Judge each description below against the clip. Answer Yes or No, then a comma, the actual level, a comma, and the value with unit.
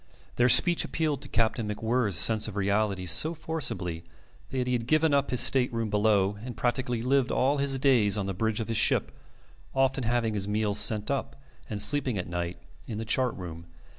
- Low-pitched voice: Yes, low, 115 Hz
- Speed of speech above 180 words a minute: Yes, average, 195 wpm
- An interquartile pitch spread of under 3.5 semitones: No, average, 4.2 semitones